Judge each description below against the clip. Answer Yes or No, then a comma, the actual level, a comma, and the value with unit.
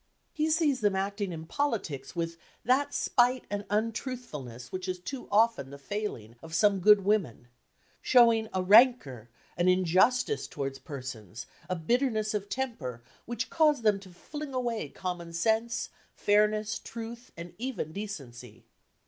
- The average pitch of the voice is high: Yes, high, 205 Hz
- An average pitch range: No, wide, 6.5 semitones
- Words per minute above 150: No, average, 140 wpm